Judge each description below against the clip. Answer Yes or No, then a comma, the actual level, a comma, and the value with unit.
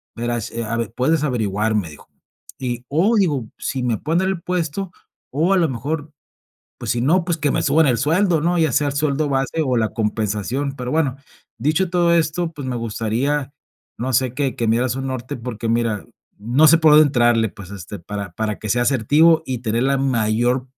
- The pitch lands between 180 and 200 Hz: No, low, 130 Hz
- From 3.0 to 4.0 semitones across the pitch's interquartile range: No, average, 5.1 semitones